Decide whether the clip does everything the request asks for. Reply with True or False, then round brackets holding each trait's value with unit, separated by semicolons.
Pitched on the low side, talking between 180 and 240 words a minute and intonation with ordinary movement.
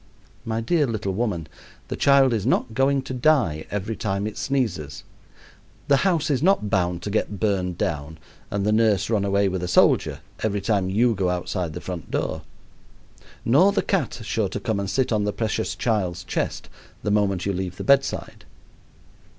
True (105 Hz; 185 wpm; 4.6 semitones)